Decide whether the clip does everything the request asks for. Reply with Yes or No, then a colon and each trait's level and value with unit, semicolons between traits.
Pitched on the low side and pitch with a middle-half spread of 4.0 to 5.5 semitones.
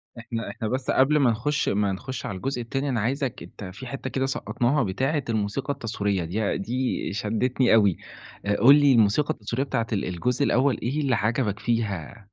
Yes: low, 120 Hz; average, 4.3 semitones